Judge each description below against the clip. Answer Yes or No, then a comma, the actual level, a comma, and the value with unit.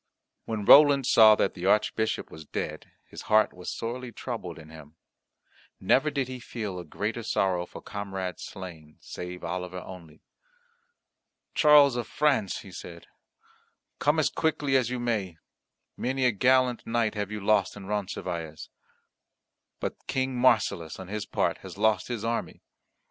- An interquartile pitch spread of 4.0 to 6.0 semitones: Yes, wide, 5.4 semitones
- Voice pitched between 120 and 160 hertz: No, low, 105 Hz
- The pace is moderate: Yes, average, 150 wpm